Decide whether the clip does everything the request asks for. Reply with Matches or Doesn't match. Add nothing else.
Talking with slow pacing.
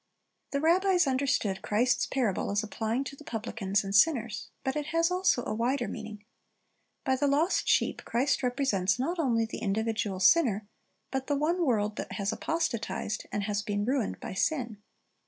Doesn't match